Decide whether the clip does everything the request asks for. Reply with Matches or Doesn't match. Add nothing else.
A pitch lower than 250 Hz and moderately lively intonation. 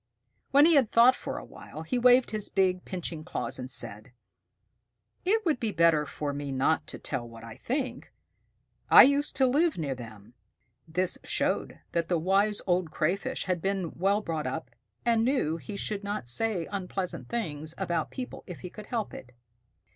Doesn't match